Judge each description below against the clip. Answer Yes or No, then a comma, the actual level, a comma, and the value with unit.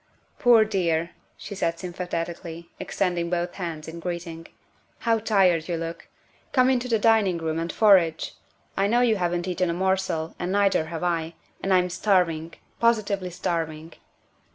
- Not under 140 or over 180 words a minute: Yes, average, 160 wpm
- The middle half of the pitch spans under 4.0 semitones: Yes, average, 3.0 semitones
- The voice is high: No, medium, 175 Hz